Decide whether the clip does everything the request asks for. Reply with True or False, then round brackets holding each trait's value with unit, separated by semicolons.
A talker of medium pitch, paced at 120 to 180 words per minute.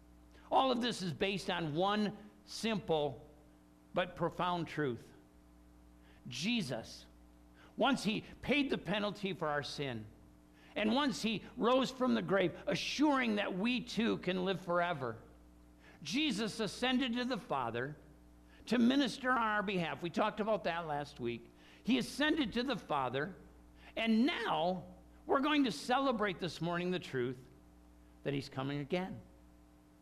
True (175 Hz; 140 wpm)